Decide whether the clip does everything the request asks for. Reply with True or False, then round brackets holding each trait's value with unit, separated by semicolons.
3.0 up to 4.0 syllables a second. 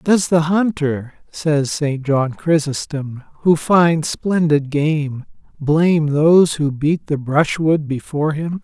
True (3.5 syllables/s)